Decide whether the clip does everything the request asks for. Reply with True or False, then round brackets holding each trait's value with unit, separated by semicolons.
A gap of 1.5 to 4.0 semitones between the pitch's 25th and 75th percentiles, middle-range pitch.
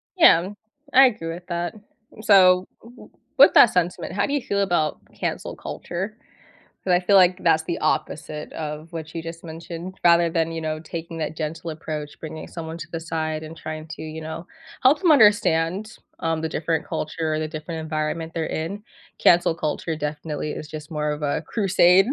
True (2.4 semitones; 165 Hz)